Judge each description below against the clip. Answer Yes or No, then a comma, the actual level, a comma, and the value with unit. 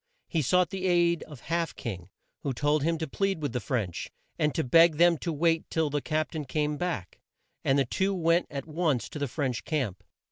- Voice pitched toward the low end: No, medium, 155 Hz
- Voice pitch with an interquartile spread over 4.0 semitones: No, average, 3.6 semitones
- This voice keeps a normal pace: No, fast, 215 wpm